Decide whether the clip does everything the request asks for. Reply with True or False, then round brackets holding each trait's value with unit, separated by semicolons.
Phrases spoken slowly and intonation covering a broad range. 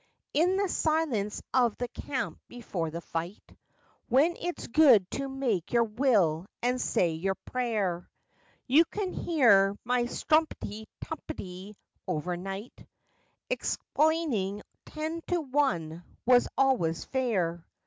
True (115 wpm; 7.0 semitones)